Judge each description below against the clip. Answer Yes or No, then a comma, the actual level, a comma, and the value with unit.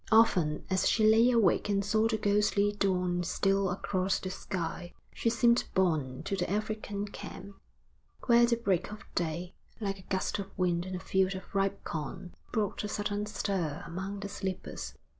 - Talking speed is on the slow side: No, average, 175 wpm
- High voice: Yes, high, 195 Hz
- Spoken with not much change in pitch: Yes, narrow, 2.3 semitones